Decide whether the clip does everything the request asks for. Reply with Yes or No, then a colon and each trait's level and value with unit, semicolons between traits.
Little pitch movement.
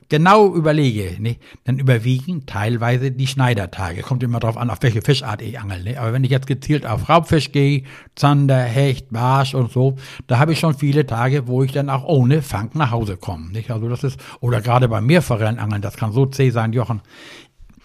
No: average, 3.1 semitones